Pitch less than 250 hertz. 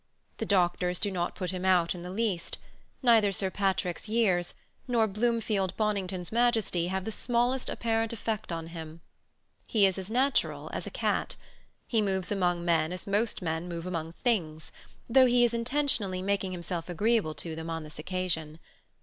Yes: high, 190 Hz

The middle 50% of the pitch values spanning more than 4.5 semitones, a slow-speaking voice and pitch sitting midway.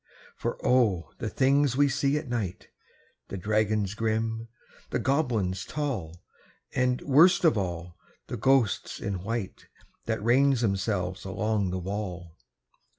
No: average, 5.3 semitones; slow, 130 wpm; low, 110 Hz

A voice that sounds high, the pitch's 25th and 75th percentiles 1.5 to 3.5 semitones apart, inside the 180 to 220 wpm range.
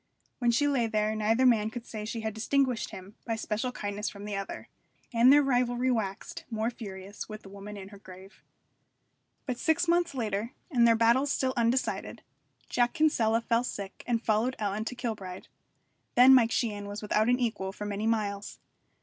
Yes: high, 225 Hz; average, 2.9 semitones; average, 185 wpm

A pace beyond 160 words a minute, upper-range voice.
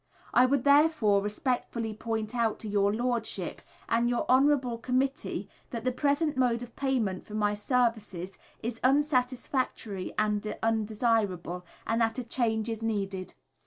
No: average, 140 wpm; high, 230 Hz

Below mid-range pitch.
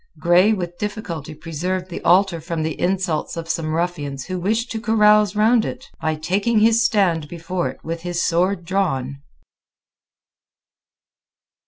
No: medium, 175 Hz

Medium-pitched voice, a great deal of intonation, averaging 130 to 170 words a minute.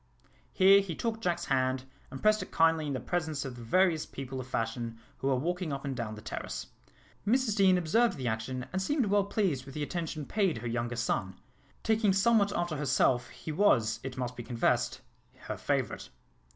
No: medium, 150 Hz; wide, 7.3 semitones; average, 190 wpm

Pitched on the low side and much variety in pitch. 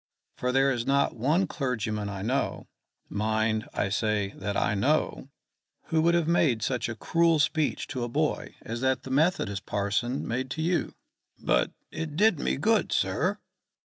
Yes: low, 130 Hz; wide, 6.1 semitones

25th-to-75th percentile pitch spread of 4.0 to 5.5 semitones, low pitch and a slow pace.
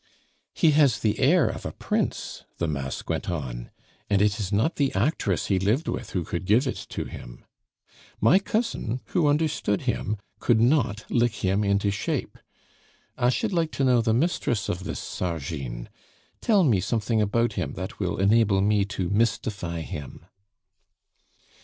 No: average, 5.1 semitones; low, 105 Hz; average, 165 wpm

